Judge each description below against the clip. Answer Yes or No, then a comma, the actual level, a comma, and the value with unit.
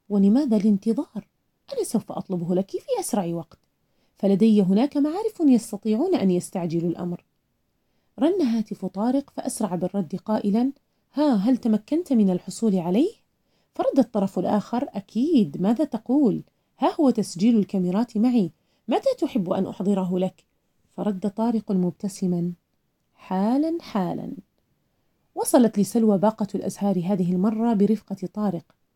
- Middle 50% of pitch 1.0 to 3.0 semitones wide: No, average, 4.5 semitones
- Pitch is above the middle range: Yes, high, 210 Hz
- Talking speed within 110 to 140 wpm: Yes, average, 120 wpm